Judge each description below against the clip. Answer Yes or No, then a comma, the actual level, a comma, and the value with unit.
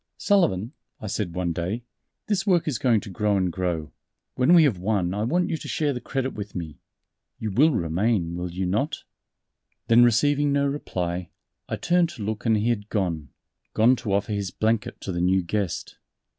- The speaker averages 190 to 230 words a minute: Yes, average, 195 wpm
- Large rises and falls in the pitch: Yes, wide, 6.3 semitones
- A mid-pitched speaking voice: No, low, 105 Hz